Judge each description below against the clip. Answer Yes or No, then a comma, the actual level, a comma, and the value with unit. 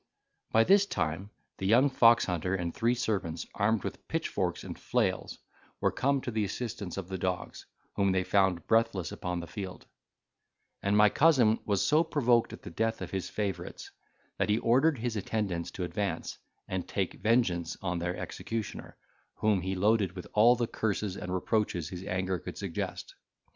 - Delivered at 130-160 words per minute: No, average, 170 wpm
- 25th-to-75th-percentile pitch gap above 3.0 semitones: Yes, average, 3.9 semitones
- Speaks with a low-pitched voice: Yes, low, 100 Hz